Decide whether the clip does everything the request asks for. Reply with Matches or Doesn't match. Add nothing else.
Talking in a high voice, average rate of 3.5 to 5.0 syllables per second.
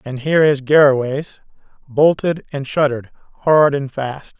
Doesn't match